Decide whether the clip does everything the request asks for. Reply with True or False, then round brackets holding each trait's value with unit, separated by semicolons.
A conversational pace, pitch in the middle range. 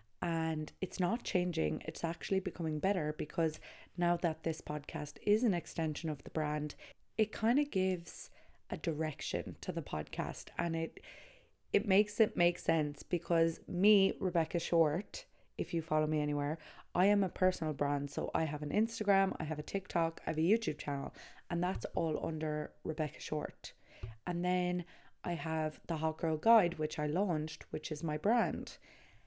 True (170 wpm; 165 Hz)